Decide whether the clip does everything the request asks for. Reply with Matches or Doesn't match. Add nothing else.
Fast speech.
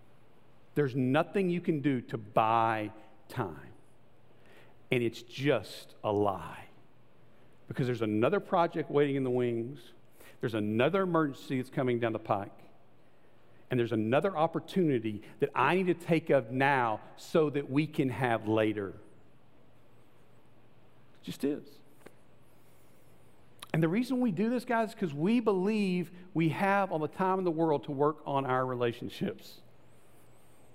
Doesn't match